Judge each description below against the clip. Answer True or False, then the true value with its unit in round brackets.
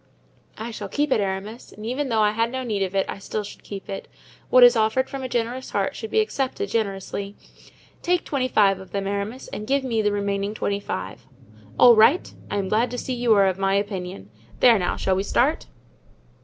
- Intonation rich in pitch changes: False (4.0 semitones)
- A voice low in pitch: False (215 Hz)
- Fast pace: True (220 wpm)